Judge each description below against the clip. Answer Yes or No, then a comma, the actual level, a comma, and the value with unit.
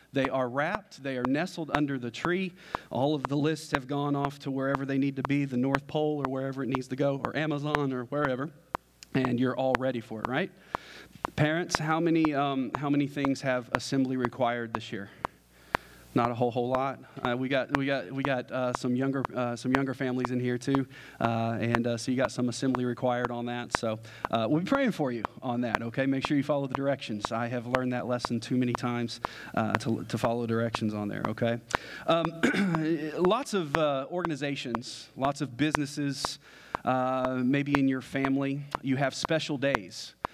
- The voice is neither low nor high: No, low, 130 Hz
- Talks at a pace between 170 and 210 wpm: Yes, average, 200 wpm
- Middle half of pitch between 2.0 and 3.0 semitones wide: Yes, average, 2.7 semitones